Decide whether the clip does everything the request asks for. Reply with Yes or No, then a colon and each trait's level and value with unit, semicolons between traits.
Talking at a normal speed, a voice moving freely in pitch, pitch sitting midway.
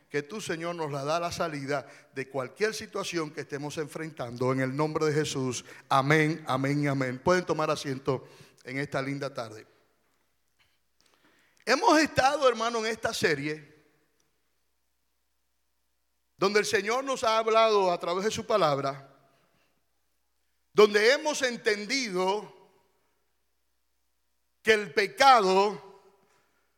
No: slow, 120 wpm; wide, 7.0 semitones; medium, 155 Hz